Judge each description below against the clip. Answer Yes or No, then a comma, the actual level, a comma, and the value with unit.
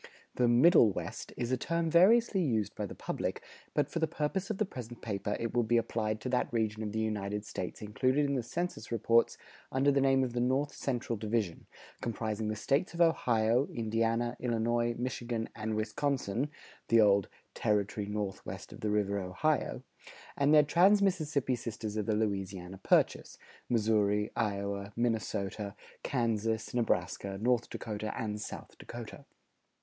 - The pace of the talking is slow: No, average, 160 wpm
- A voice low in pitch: Yes, low, 115 Hz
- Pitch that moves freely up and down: No, average, 3.8 semitones